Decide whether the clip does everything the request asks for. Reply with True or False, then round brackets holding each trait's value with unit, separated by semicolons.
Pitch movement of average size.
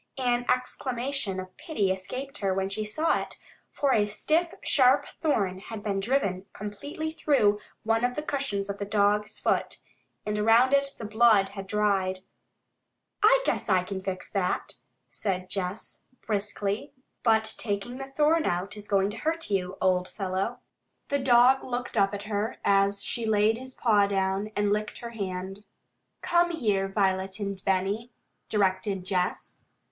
True (4.1 semitones)